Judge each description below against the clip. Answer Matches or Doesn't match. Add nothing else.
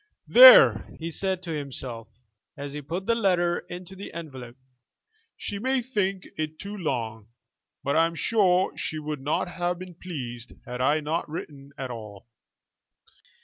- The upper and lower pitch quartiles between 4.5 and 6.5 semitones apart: Matches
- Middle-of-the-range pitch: Matches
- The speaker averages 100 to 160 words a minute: Matches